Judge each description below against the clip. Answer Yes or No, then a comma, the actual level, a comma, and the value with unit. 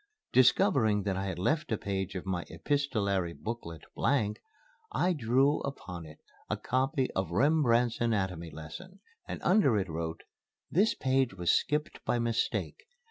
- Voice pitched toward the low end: Yes, low, 115 Hz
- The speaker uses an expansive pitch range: Yes, wide, 6.7 semitones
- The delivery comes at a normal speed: Yes, average, 145 wpm